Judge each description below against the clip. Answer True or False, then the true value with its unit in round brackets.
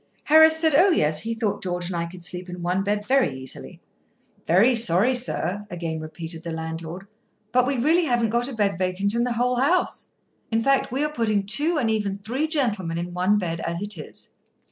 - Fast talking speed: True (210 wpm)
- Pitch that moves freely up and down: True (6.1 semitones)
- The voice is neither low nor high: False (205 Hz)